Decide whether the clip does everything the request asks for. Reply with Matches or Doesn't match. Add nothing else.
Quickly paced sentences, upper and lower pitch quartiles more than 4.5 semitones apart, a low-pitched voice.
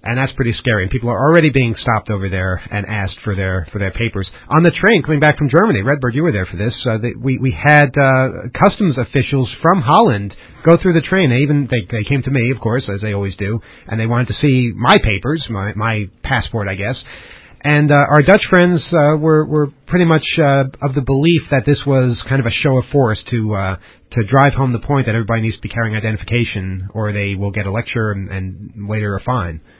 Matches